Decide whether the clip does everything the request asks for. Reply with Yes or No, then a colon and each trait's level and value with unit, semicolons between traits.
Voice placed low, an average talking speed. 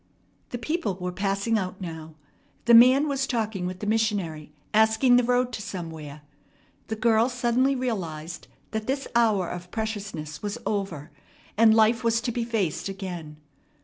No: high, 215 Hz; average, 155 wpm